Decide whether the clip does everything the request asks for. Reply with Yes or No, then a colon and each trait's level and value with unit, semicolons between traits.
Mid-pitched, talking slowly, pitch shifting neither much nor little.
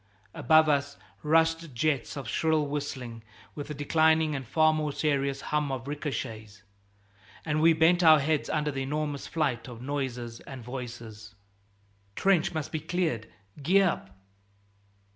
No: medium, 145 Hz; average, 145 wpm; average, 3.8 semitones